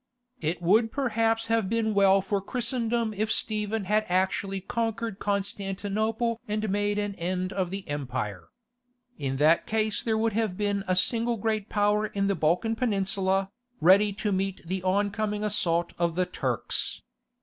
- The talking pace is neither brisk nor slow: Yes, average, 155 wpm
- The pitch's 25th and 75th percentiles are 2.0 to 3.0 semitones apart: Yes, narrow, 2.6 semitones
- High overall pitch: Yes, high, 205 Hz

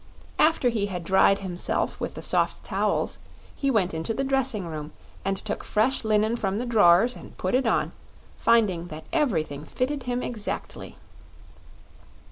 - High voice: Yes, high, 215 Hz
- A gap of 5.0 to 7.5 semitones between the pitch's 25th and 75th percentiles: Yes, wide, 5.5 semitones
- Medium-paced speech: Yes, average, 155 wpm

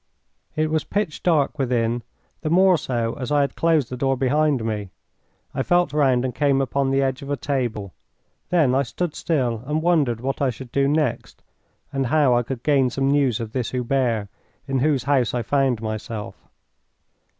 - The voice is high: No, low, 135 Hz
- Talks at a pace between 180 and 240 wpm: Yes, average, 185 wpm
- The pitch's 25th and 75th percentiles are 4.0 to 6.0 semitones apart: No, average, 3.3 semitones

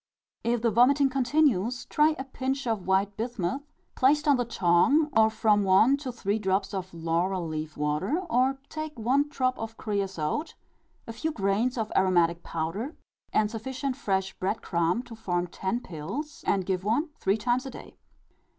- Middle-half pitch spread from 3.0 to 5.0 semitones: No, wide, 5.6 semitones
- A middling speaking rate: Yes, average, 170 wpm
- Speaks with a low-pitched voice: No, high, 220 Hz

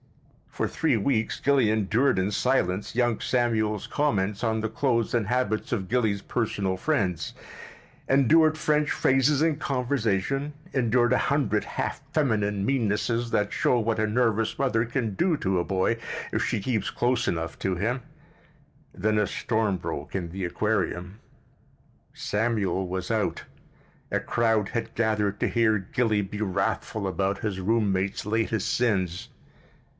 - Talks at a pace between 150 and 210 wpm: No, average, 140 wpm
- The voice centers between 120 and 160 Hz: No, low, 110 Hz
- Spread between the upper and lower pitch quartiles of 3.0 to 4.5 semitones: Yes, average, 3.8 semitones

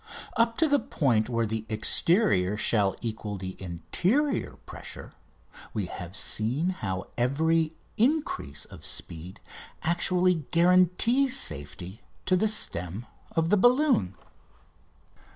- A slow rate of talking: Yes, slow, 115 wpm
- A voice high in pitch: No, medium, 140 Hz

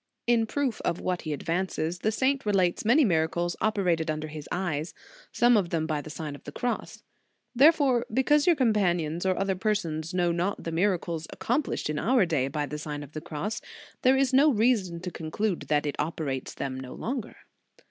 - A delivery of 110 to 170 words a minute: No, average, 195 wpm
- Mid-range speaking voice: Yes, medium, 180 Hz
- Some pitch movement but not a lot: No, wide, 6.4 semitones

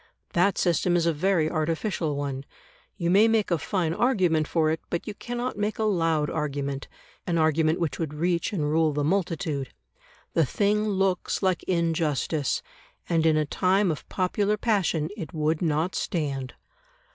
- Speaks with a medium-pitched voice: Yes, medium, 165 Hz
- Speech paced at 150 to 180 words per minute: Yes, average, 165 wpm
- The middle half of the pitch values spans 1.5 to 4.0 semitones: Yes, average, 3.7 semitones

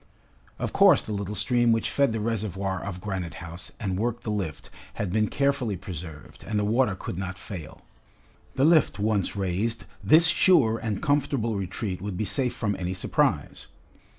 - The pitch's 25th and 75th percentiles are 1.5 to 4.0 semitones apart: Yes, average, 3.7 semitones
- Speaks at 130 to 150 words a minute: No, average, 175 wpm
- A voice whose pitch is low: Yes, low, 105 Hz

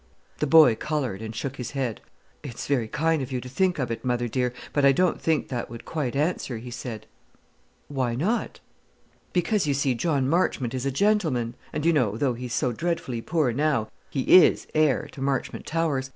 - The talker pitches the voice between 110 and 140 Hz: Yes, low, 135 Hz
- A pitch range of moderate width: Yes, average, 4.1 semitones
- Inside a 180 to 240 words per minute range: Yes, average, 195 wpm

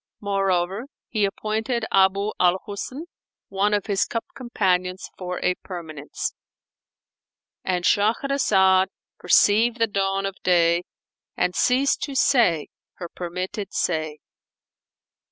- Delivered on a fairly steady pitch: No, average, 3.0 semitones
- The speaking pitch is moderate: No, high, 195 Hz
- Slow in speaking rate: Yes, slow, 105 wpm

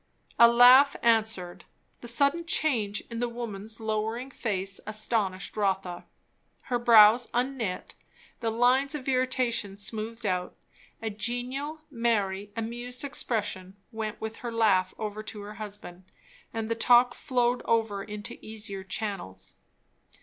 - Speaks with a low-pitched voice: No, high, 225 Hz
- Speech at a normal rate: No, slow, 130 wpm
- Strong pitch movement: No, average, 2.9 semitones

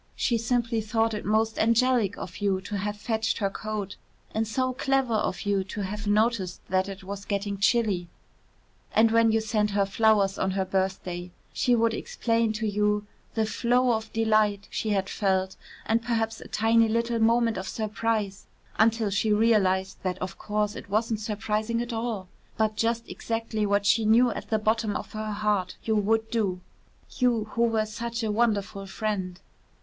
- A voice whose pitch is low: No, high, 215 Hz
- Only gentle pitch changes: Yes, narrow, 2.2 semitones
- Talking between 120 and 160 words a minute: No, average, 175 wpm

